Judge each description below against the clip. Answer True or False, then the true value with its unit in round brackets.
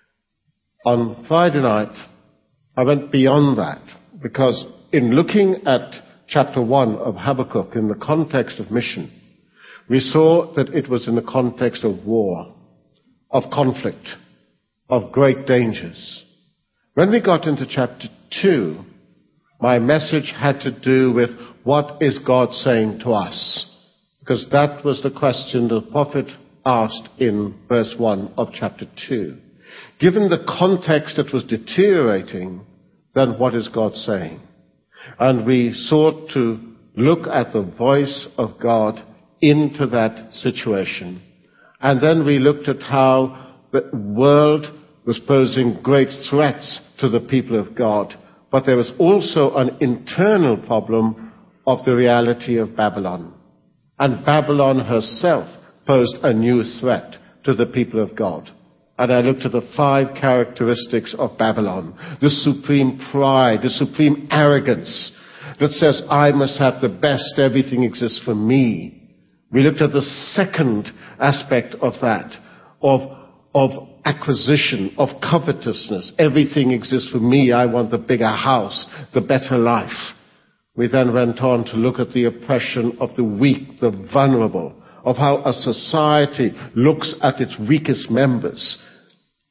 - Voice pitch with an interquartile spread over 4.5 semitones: False (3.2 semitones)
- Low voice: True (130 Hz)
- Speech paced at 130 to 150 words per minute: True (140 wpm)